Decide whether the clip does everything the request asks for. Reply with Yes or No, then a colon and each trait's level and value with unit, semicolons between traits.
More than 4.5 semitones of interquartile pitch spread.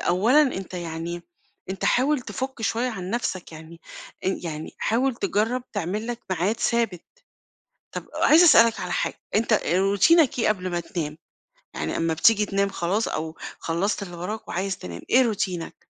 Yes: average, 5.1 semitones